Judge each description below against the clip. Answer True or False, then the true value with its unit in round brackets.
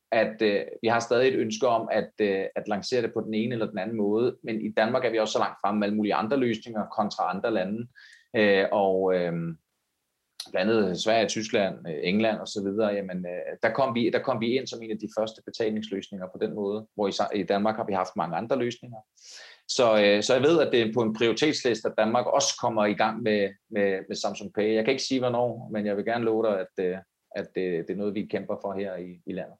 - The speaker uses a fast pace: True (240 wpm)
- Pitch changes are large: False (2.5 semitones)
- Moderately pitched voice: False (105 Hz)